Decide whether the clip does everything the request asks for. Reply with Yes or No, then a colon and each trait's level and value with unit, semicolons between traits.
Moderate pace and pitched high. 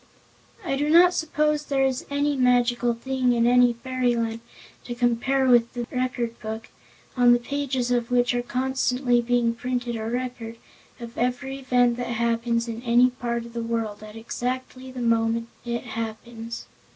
Yes: average, 165 wpm; high, 245 Hz